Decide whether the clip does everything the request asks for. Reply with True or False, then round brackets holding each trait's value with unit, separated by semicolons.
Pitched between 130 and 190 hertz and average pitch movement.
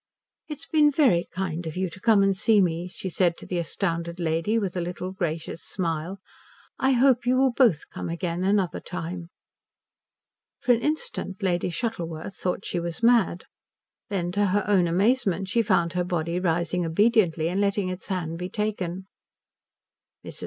True (185 Hz; 3.5 semitones)